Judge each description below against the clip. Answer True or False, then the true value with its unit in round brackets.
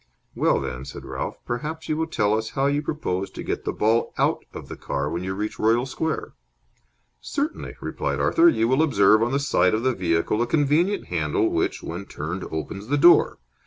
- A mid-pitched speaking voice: False (115 Hz)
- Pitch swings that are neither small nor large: False (7.9 semitones)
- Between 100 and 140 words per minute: False (200 wpm)